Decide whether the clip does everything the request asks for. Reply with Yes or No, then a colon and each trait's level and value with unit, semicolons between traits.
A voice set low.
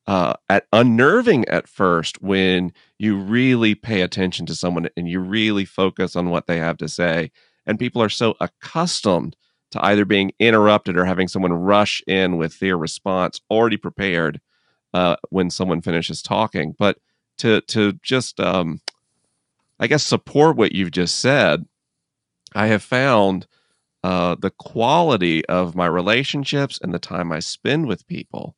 Yes: very low, 95 Hz